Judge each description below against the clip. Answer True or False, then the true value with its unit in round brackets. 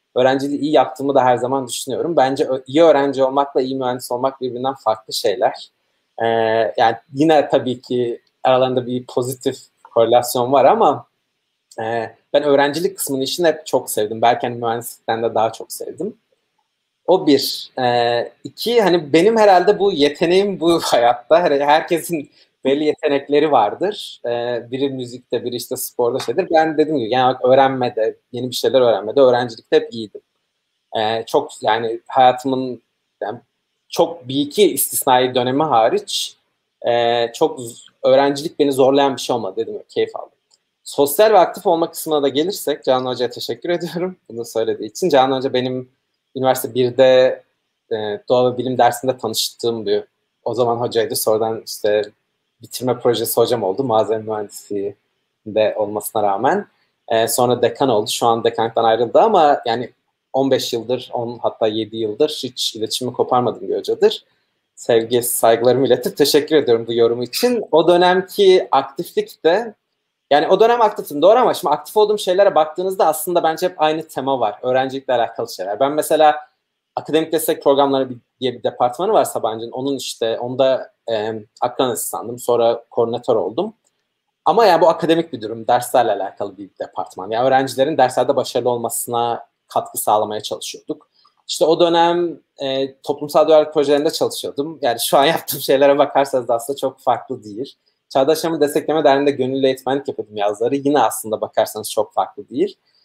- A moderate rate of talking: False (150 wpm)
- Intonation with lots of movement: False (4.5 semitones)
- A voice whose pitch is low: True (130 Hz)